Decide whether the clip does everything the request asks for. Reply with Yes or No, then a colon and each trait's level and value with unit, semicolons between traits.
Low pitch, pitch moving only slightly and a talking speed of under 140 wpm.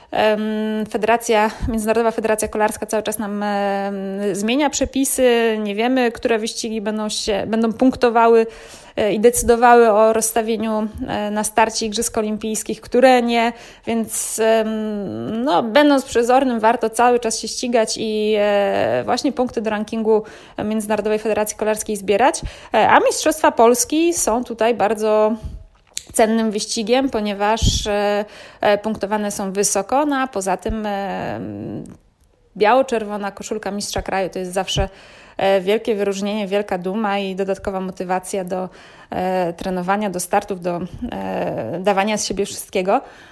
No: high, 215 Hz; narrow, 2.2 semitones; average, 115 wpm